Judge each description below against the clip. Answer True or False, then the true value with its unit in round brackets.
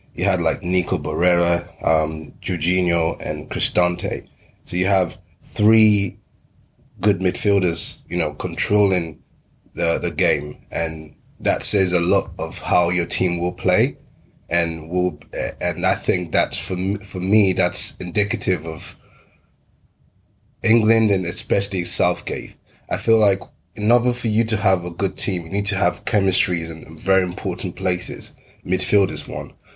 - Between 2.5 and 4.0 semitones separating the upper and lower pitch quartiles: True (3.0 semitones)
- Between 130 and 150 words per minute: True (145 wpm)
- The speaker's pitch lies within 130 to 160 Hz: False (95 Hz)